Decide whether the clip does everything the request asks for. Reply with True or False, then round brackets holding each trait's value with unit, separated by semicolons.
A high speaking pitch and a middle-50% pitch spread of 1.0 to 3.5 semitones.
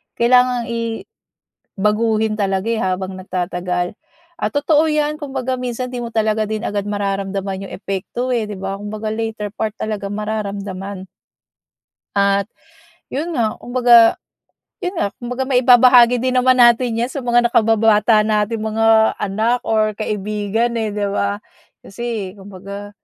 True (220 Hz; 3.1 semitones)